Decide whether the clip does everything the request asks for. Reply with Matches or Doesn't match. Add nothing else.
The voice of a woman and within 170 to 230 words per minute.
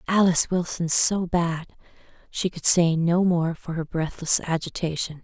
Doesn't match